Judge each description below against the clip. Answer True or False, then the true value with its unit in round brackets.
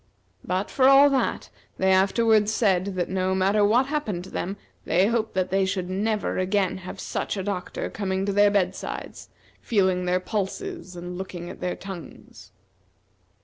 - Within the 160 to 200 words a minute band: True (170 wpm)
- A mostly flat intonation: True (2.3 semitones)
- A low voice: False (190 Hz)